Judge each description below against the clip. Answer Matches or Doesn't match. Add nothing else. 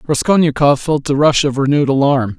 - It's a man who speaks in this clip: Matches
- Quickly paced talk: Doesn't match